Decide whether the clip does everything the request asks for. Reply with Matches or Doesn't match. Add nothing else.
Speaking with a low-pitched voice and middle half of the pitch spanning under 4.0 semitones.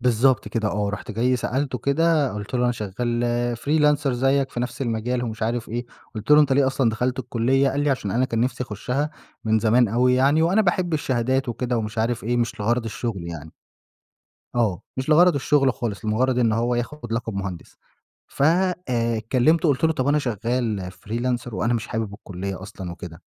Matches